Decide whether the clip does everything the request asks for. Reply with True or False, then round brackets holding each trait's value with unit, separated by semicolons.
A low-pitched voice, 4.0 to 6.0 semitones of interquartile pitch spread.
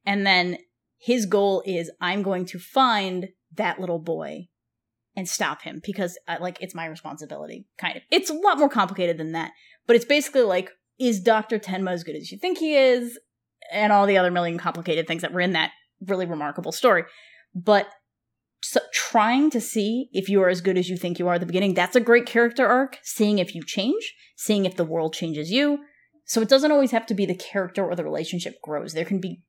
False (190 Hz; 5.3 semitones)